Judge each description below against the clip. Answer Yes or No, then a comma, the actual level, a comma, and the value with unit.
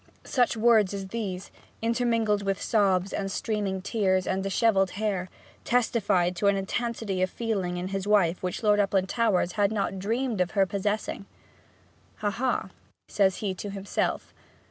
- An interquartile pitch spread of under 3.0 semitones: Yes, narrow, 2.6 semitones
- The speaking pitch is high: Yes, high, 200 Hz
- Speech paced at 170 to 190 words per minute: No, average, 150 wpm